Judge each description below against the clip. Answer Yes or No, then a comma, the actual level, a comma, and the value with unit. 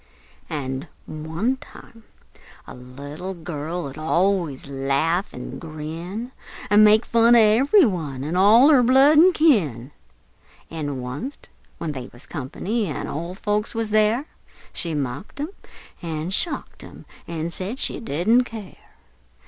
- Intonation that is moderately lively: No, wide, 7.2 semitones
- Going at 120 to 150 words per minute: Yes, average, 140 wpm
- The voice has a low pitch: No, medium, 175 Hz